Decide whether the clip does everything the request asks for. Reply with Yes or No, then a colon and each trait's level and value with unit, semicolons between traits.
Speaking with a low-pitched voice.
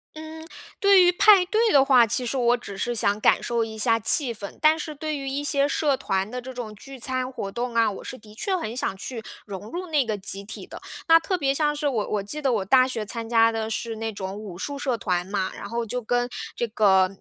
No: high, 240 Hz